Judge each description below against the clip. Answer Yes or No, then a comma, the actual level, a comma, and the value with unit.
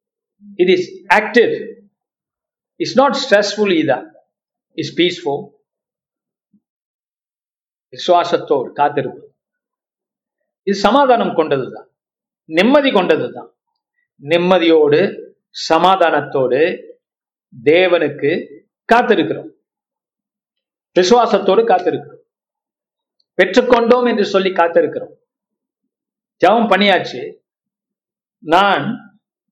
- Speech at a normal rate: No, slow, 45 wpm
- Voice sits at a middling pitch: No, high, 230 Hz